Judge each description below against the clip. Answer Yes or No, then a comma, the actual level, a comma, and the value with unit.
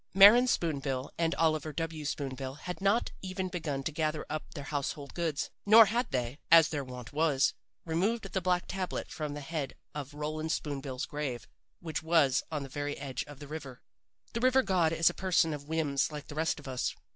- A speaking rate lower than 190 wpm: No, fast, 205 wpm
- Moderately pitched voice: Yes, medium, 155 Hz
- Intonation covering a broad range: No, average, 3.4 semitones